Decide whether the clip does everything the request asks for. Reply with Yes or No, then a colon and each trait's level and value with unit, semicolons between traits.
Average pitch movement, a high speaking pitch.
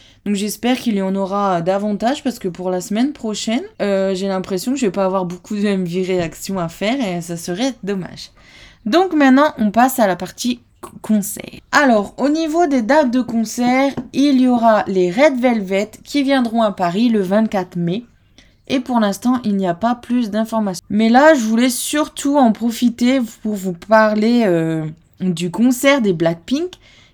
Yes: average, 4.8 semitones; high, 220 Hz